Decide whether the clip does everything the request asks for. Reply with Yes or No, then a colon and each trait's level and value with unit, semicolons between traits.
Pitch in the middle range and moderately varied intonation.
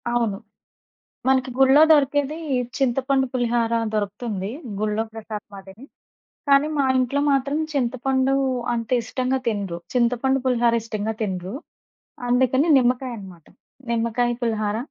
No: high, 240 Hz; average, 3.5 semitones